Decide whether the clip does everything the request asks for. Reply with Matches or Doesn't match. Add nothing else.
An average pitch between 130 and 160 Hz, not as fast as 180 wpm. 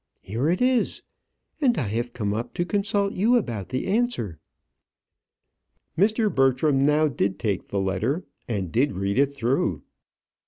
Matches